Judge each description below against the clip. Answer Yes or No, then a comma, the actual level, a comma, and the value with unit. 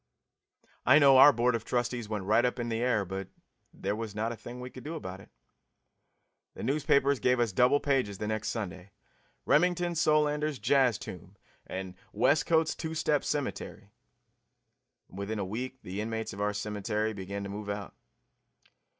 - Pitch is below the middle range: Yes, low, 115 Hz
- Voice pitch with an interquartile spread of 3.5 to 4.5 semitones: No, average, 5.1 semitones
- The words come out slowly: No, average, 170 wpm